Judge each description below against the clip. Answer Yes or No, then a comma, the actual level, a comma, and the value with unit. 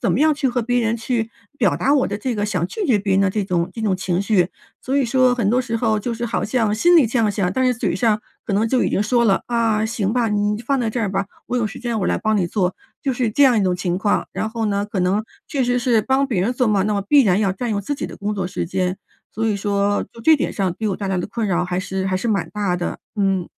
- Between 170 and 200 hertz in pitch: No, high, 215 Hz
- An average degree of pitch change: Yes, average, 3.7 semitones